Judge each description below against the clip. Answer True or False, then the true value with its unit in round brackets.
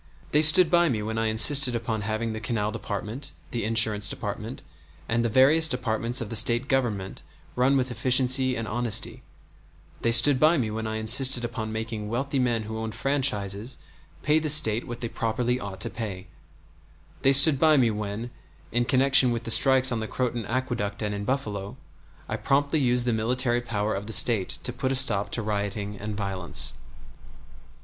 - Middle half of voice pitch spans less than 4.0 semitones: True (3.1 semitones)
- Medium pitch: False (115 Hz)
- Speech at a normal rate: True (185 wpm)